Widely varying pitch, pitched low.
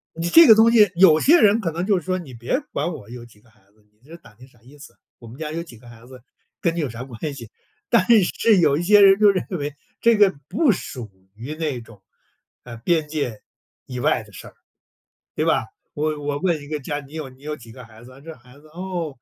No: wide, 6.3 semitones; medium, 150 Hz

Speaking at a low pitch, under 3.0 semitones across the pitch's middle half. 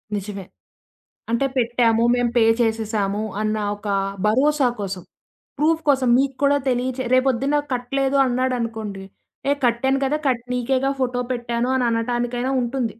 No: high, 245 Hz; narrow, 2.6 semitones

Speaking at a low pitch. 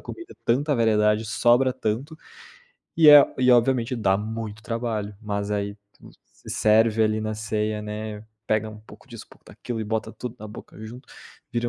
Yes: low, 110 Hz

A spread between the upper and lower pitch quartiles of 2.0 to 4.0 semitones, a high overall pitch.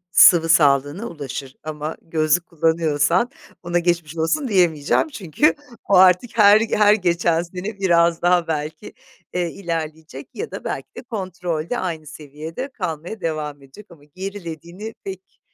No: average, 3.5 semitones; medium, 170 Hz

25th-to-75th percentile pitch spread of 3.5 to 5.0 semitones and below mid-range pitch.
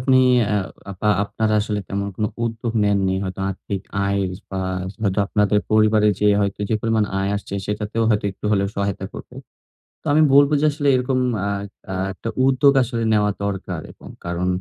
No: narrow, 2.4 semitones; low, 105 Hz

